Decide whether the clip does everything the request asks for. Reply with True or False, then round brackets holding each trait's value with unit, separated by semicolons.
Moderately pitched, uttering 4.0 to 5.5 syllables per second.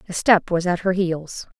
True (180 Hz; 4.6 syllables/s)